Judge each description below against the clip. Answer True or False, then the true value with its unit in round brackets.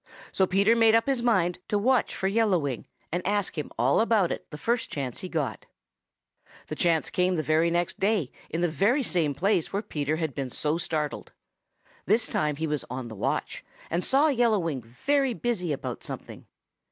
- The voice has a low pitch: False (175 Hz)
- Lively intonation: True (6.5 semitones)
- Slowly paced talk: False (195 wpm)